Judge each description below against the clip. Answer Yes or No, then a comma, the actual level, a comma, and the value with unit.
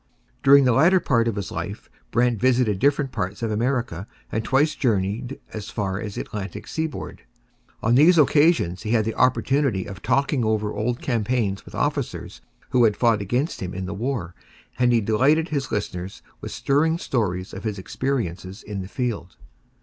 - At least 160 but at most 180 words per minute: Yes, average, 175 wpm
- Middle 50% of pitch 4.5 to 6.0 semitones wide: Yes, average, 5.0 semitones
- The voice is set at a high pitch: No, low, 115 Hz